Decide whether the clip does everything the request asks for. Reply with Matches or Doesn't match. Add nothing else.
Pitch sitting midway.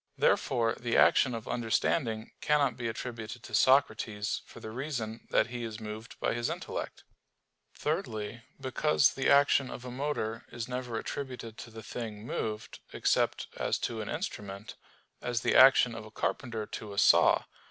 Doesn't match